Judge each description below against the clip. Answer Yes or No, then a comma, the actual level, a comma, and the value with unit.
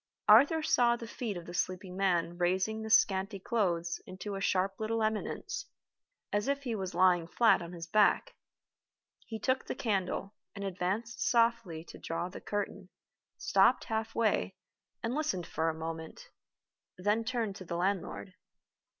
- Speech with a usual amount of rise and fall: Yes, average, 4.1 semitones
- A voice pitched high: Yes, high, 200 Hz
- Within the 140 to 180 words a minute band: Yes, average, 160 wpm